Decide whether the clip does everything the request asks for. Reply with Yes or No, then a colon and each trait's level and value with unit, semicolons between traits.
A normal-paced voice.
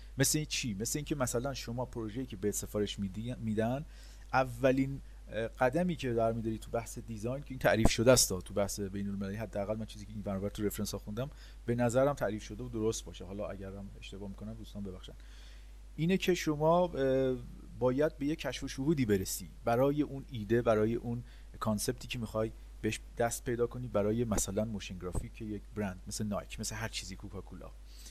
No: fast, 185 wpm